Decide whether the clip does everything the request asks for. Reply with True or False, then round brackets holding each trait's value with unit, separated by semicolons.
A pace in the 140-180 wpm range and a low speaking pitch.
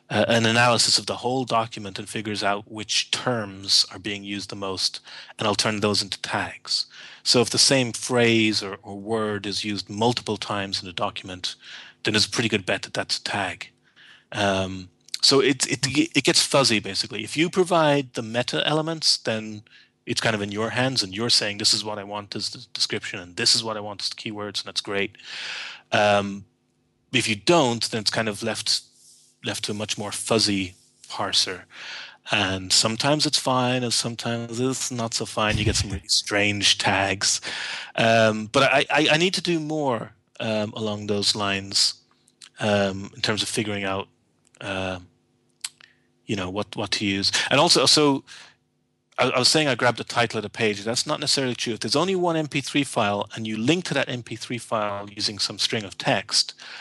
False (195 wpm; 110 Hz)